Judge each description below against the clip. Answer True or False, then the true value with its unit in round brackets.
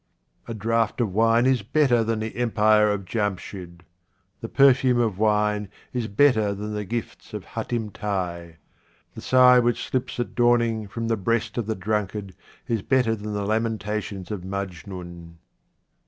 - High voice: False (110 Hz)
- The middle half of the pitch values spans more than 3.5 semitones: False (2.8 semitones)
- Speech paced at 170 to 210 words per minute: False (155 wpm)